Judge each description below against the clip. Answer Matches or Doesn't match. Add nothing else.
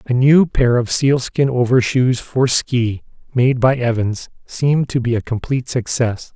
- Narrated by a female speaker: Doesn't match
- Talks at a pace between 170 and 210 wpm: Doesn't match